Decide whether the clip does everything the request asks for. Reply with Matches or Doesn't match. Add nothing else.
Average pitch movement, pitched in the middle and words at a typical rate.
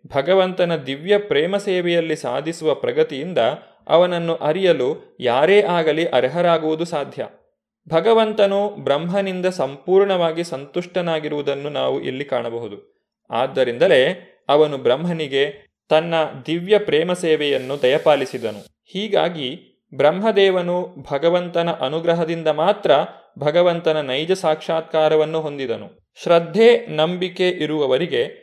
Matches